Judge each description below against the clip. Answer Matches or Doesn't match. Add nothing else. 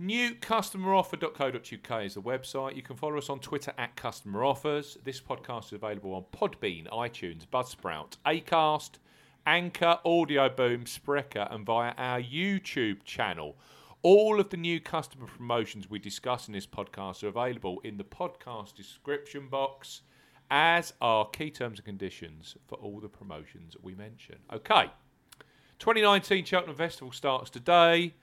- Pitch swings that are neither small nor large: Doesn't match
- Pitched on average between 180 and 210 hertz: Doesn't match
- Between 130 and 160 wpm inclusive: Matches